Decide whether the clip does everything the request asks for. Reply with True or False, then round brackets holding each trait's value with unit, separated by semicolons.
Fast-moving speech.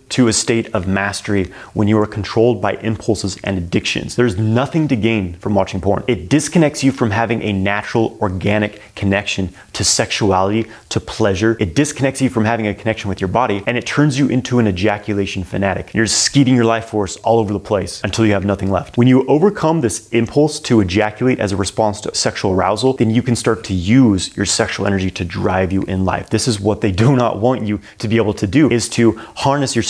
True (220 wpm)